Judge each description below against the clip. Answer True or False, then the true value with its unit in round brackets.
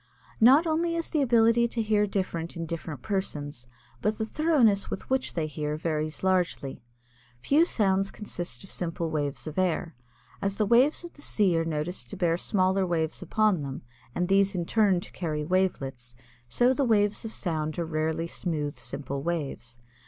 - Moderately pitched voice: True (180 Hz)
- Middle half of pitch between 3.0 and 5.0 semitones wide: False (5.5 semitones)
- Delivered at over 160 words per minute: True (175 wpm)